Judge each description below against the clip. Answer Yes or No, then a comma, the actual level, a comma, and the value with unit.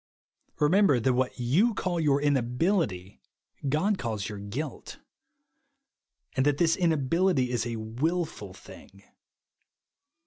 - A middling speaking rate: No, slow, 115 wpm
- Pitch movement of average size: No, wide, 6.0 semitones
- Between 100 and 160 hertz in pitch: Yes, medium, 140 Hz